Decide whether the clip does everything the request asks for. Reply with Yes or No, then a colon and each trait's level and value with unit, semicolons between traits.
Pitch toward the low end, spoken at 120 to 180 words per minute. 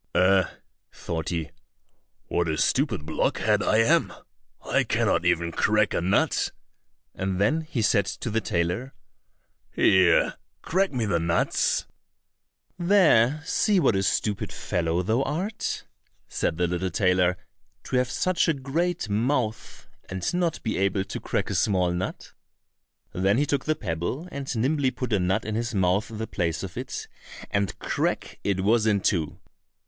Yes: low, 105 Hz; average, 155 wpm